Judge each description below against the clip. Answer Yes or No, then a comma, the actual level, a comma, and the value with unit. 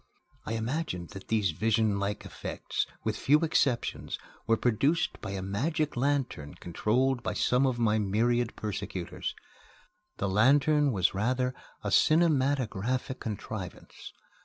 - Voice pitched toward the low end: Yes, low, 115 Hz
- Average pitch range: Yes, average, 4.8 semitones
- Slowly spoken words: Yes, slow, 120 wpm